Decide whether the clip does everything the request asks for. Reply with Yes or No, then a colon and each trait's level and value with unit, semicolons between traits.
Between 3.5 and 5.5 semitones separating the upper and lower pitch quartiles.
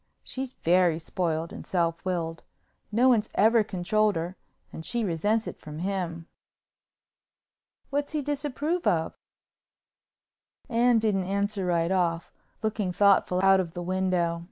Yes: average, 4.4 semitones